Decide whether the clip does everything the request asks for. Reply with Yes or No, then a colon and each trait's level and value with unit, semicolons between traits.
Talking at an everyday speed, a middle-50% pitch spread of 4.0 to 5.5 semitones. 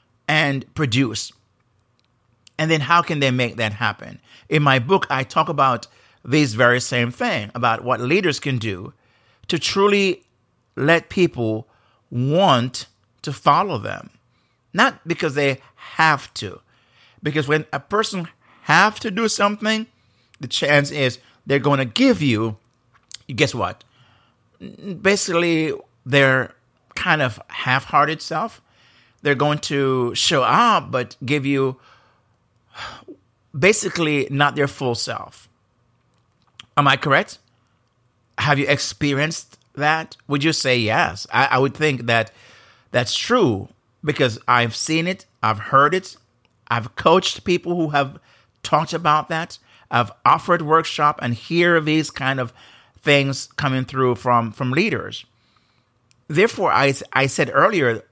No: slow, 130 wpm; average, 4.4 semitones